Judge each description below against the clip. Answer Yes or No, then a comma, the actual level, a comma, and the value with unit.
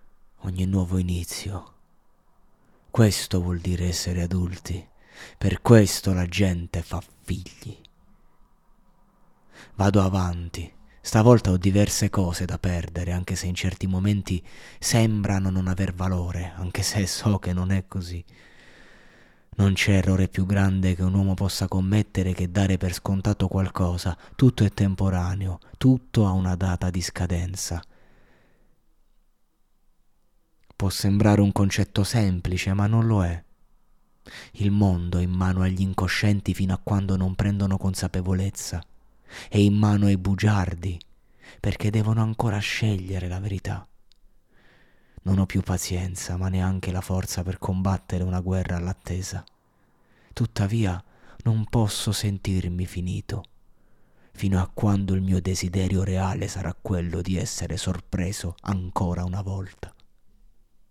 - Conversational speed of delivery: Yes, average, 125 wpm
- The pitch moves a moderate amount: No, narrow, 1.8 semitones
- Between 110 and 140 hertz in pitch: No, very low, 95 Hz